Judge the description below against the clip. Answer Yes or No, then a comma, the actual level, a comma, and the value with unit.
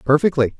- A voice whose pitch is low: No, medium, 145 Hz